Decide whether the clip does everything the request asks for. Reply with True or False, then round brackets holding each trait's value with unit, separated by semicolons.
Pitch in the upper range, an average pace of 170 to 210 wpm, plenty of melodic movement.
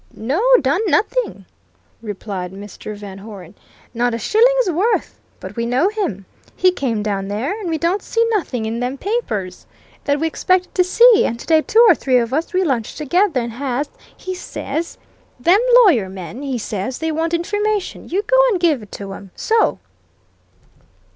True (285 Hz; 175 wpm; 8.9 semitones)